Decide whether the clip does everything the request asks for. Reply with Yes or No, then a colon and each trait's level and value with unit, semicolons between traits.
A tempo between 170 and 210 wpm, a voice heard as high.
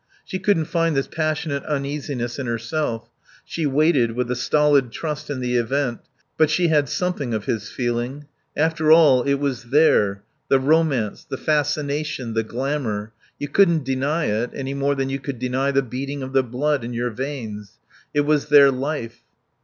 No: average, 175 wpm; medium, 140 Hz